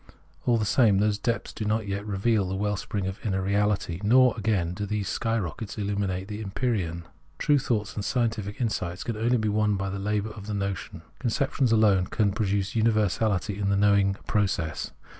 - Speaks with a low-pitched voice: Yes, low, 105 Hz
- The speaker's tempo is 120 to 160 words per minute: No, average, 190 wpm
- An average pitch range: No, narrow, 2.2 semitones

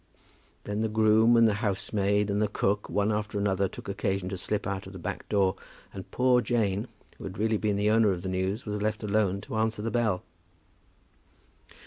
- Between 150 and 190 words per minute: No, average, 200 wpm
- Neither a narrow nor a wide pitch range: No, narrow, 1.8 semitones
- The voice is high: No, low, 105 Hz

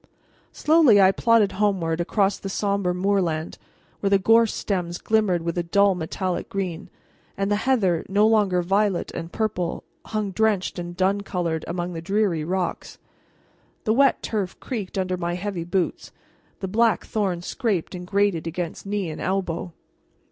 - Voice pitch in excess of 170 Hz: Yes, high, 190 Hz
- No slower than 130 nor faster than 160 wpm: Yes, average, 155 wpm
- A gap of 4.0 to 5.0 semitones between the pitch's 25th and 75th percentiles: No, average, 2.9 semitones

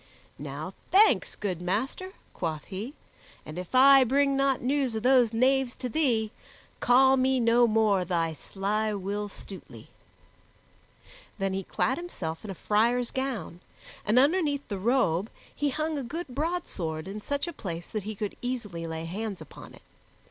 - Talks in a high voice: Yes, high, 230 Hz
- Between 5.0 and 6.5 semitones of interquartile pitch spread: Yes, wide, 5.6 semitones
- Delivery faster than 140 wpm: Yes, average, 160 wpm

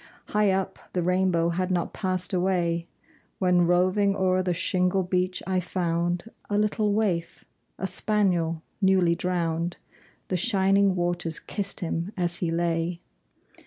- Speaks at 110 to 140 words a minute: Yes, slow, 135 wpm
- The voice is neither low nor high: Yes, medium, 180 Hz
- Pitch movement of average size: No, narrow, 1.9 semitones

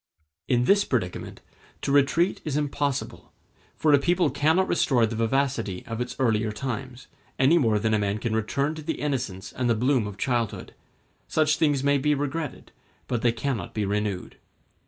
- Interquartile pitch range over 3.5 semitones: Yes, average, 4.6 semitones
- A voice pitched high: No, low, 130 Hz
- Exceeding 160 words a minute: Yes, average, 175 wpm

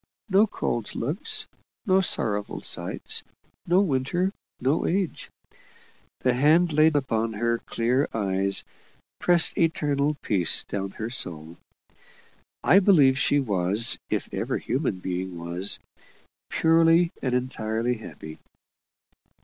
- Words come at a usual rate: No, slow, 115 wpm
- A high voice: No, low, 130 Hz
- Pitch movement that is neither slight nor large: No, wide, 7.8 semitones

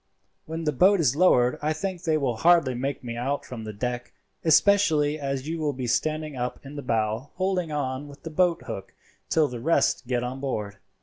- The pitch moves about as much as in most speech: Yes, average, 4.6 semitones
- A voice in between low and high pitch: Yes, medium, 145 Hz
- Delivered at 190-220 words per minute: Yes, fast, 205 wpm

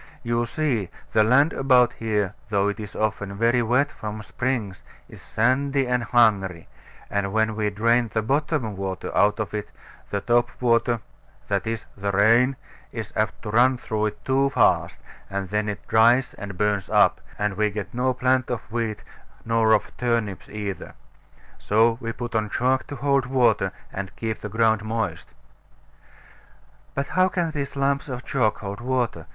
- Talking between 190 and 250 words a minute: No, average, 170 wpm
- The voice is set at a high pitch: No, low, 115 Hz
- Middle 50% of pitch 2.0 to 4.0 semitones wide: Yes, average, 3.2 semitones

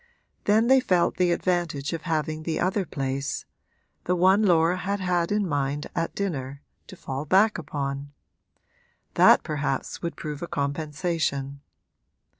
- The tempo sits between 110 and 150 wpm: Yes, average, 140 wpm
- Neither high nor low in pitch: Yes, medium, 165 Hz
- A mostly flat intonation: No, average, 4.3 semitones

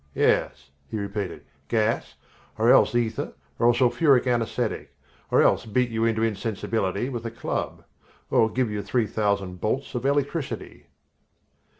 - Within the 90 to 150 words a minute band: Yes, average, 140 wpm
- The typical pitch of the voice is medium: No, low, 115 Hz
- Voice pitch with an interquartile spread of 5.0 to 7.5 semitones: No, average, 2.7 semitones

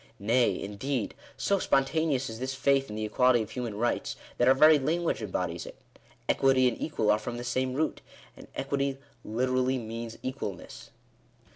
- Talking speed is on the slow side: No, average, 170 wpm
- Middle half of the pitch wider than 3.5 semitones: No, average, 3.2 semitones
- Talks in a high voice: No, low, 130 Hz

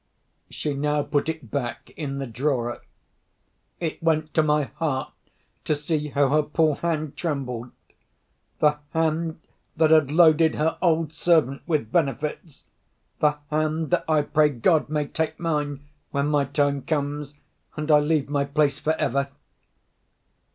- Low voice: No, medium, 150 Hz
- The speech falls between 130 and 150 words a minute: Yes, average, 145 wpm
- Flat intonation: Yes, narrow, 2.0 semitones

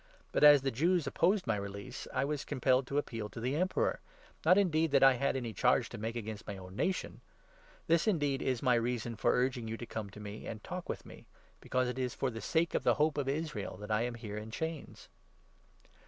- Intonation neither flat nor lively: Yes, average, 5.0 semitones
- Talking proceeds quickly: Yes, fast, 240 wpm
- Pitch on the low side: Yes, low, 130 Hz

